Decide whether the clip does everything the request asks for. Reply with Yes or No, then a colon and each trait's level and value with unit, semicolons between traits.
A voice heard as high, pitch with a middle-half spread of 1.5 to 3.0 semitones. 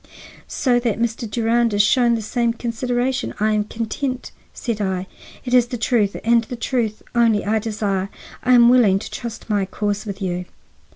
Yes: high, 230 Hz; narrow, 2.6 semitones